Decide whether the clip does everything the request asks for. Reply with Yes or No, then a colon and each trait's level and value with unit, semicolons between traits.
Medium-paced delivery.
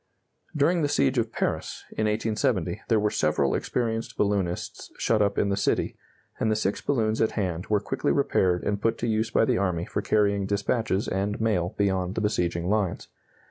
Yes: average, 185 wpm